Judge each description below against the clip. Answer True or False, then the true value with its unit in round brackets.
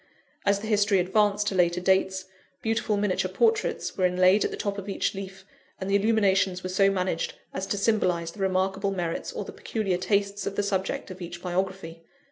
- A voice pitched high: True (195 Hz)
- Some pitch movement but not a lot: False (1.7 semitones)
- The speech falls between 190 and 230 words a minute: True (195 wpm)